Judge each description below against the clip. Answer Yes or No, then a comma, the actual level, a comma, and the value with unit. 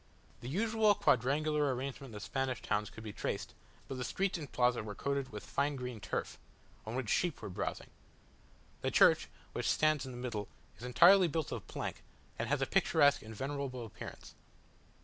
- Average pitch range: Yes, average, 4.0 semitones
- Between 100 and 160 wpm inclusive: No, average, 180 wpm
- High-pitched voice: No, low, 130 Hz